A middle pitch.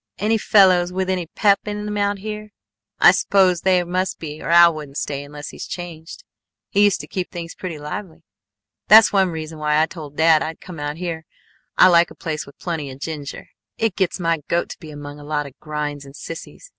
Yes: medium, 170 Hz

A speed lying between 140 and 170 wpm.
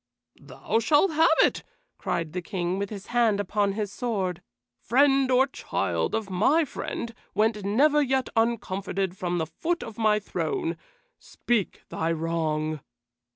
Yes: average, 145 wpm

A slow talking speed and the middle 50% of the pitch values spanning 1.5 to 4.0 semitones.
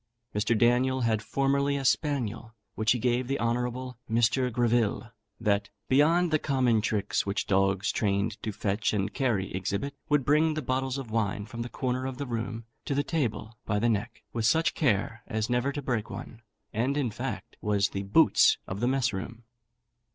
No: average, 185 wpm; average, 3.6 semitones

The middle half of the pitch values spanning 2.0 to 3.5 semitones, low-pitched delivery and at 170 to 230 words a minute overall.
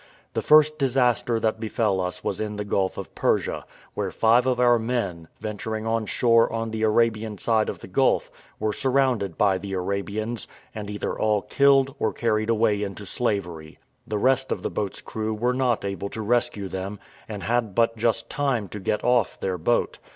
Yes: average, 2.9 semitones; low, 110 Hz; average, 190 wpm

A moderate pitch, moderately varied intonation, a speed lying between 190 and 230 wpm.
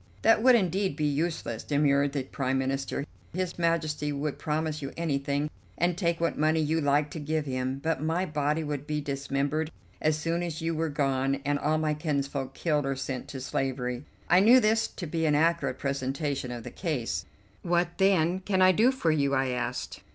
Yes: medium, 150 Hz; average, 3.3 semitones; average, 195 wpm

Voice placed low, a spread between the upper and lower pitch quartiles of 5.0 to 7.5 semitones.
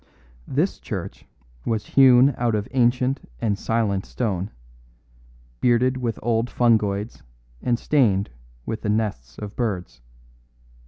No: low, 115 Hz; average, 3.3 semitones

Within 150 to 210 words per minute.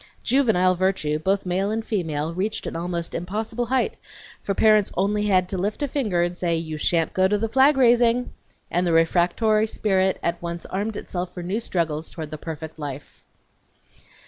Yes: average, 180 wpm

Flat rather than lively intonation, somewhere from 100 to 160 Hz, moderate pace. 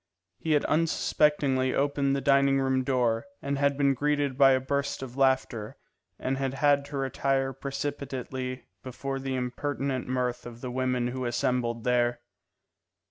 Yes: narrow, 1.7 semitones; low, 135 Hz; average, 155 wpm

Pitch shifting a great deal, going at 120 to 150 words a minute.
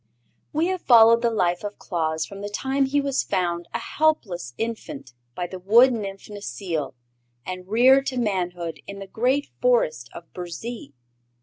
No: wide, 6.4 semitones; average, 165 wpm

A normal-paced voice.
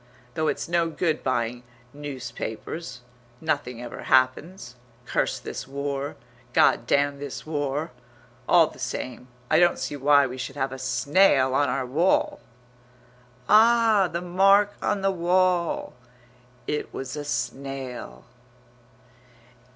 No: slow, 125 wpm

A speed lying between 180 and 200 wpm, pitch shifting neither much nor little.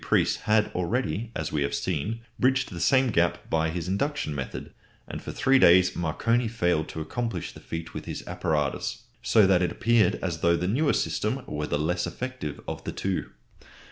No: average, 190 wpm; wide, 6.2 semitones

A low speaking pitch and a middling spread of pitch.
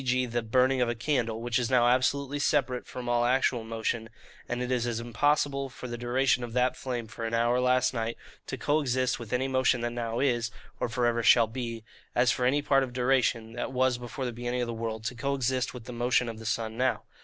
No: low, 125 Hz; narrow, 1.7 semitones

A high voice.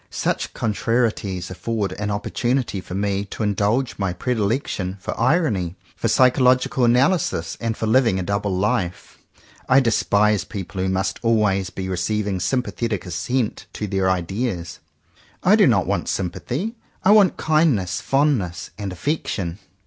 No: low, 105 Hz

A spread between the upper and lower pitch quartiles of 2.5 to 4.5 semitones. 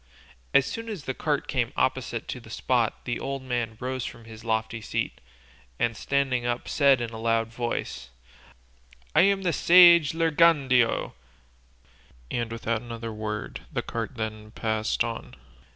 Yes: average, 3.6 semitones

